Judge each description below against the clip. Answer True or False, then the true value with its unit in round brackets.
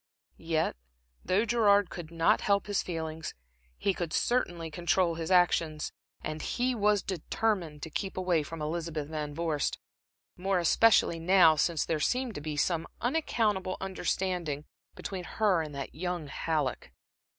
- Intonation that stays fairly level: False (3.8 semitones)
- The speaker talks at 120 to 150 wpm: True (145 wpm)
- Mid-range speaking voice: True (175 Hz)